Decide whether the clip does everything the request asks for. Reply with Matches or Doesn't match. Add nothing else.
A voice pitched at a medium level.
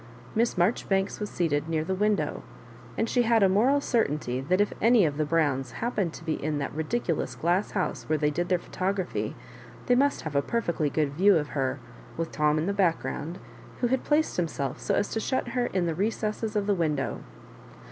Matches